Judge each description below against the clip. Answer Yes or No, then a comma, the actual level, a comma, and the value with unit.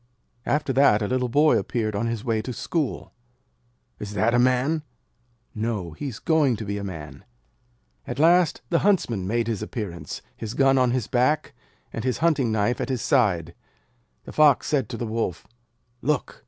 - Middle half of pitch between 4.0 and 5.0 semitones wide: Yes, average, 4.4 semitones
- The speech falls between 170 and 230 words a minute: Yes, average, 180 wpm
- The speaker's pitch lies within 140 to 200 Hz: No, low, 120 Hz